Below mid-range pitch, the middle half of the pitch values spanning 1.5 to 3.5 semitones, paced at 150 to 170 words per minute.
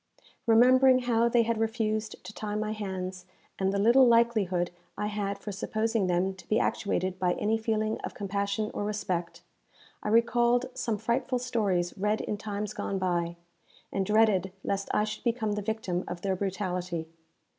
No: high, 210 Hz; average, 3.0 semitones; average, 165 wpm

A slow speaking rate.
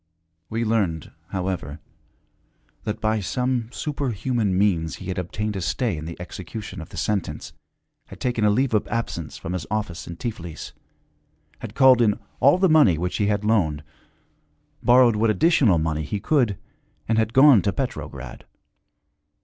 No: average, 155 wpm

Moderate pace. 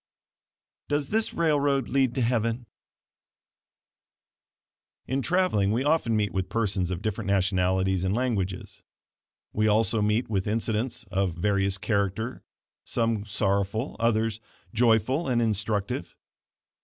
No: slow, 115 wpm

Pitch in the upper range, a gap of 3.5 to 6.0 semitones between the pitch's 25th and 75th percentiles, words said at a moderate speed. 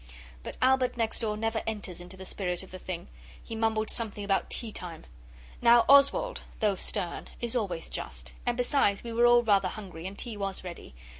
Yes: high, 215 Hz; average, 3.9 semitones; average, 195 wpm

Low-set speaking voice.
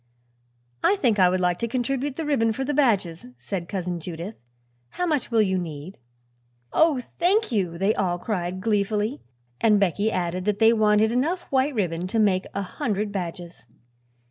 No: high, 210 Hz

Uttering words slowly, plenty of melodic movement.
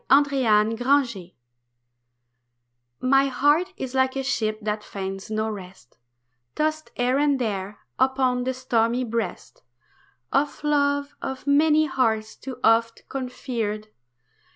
No: slow, 115 wpm; average, 4.1 semitones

